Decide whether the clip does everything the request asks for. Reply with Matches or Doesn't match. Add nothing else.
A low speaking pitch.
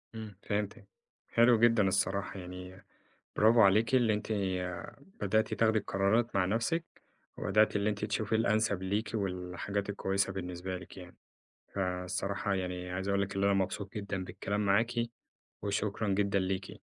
Matches